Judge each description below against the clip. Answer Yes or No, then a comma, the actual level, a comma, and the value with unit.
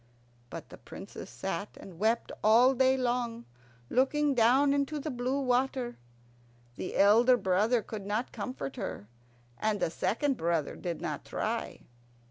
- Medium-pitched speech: No, high, 240 Hz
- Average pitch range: Yes, average, 4.0 semitones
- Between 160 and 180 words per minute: No, average, 140 wpm